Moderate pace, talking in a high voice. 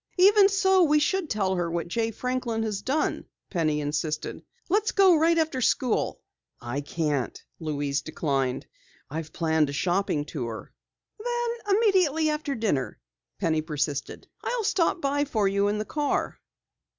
Yes: average, 145 wpm; high, 215 Hz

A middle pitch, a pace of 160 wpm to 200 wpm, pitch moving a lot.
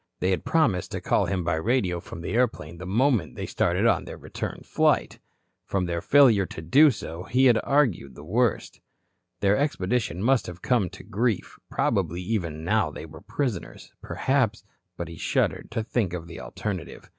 No: low, 100 Hz; average, 180 wpm; wide, 6.2 semitones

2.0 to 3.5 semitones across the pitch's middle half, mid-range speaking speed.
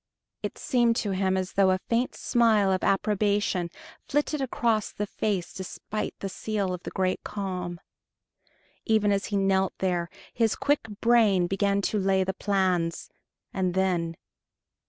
Yes: narrow, 2.5 semitones; average, 150 wpm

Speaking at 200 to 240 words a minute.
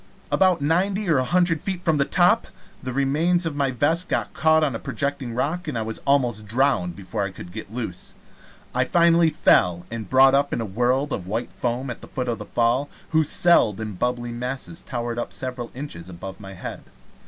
Yes: fast, 205 wpm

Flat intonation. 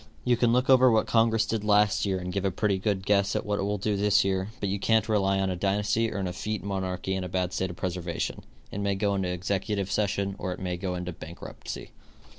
Yes: narrow, 2.0 semitones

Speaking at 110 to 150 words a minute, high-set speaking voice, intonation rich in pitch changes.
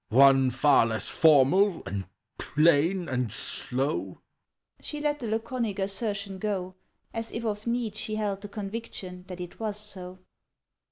Yes: average, 145 wpm; high, 195 Hz; wide, 6.5 semitones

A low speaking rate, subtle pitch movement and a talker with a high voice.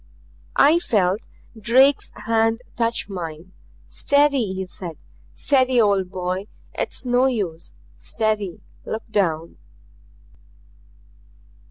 No: slow, 90 wpm; average, 5.1 semitones; high, 210 Hz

